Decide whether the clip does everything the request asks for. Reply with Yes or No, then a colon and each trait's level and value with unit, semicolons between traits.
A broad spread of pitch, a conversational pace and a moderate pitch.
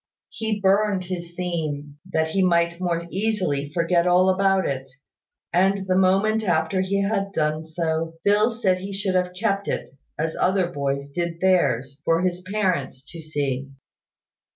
No: average, 3.3 semitones; average, 160 wpm; medium, 180 Hz